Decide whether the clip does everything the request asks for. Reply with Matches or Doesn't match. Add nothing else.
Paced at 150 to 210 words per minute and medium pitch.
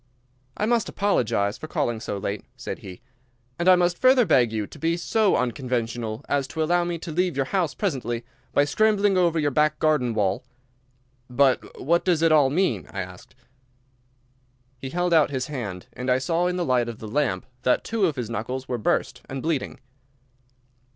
Matches